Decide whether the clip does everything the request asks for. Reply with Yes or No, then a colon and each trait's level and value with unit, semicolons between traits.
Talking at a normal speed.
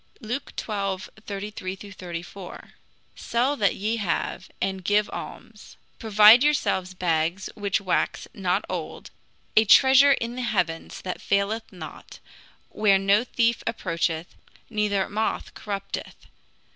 No: slow, 120 wpm